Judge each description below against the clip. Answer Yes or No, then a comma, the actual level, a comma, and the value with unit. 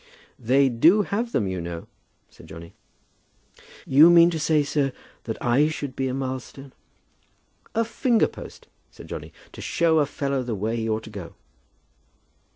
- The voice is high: No, low, 135 Hz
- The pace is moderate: Yes, average, 165 wpm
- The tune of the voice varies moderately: No, wide, 6.0 semitones